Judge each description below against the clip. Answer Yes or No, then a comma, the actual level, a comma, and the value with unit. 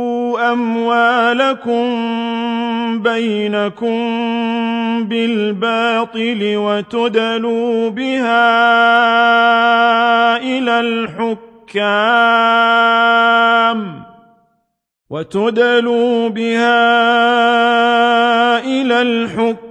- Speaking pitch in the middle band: No, high, 230 Hz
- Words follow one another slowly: Yes, slow, 35 wpm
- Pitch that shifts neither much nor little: No, narrow, 0.5 semitones